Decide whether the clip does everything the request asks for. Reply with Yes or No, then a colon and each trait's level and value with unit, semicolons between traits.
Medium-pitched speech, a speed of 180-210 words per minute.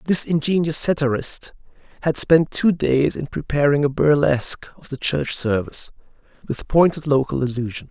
No: medium, 145 Hz; average, 145 wpm